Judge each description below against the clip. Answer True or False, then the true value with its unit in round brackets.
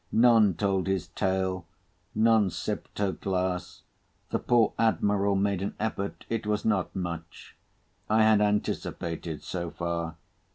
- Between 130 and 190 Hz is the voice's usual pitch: False (100 Hz)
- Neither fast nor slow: False (125 wpm)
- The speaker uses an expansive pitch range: False (2.7 semitones)